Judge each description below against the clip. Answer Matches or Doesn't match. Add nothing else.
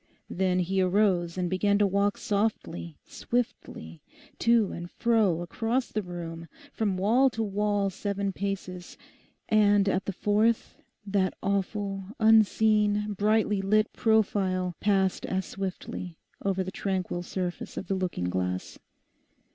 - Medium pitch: Doesn't match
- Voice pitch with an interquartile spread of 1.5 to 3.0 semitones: Matches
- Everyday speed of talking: Doesn't match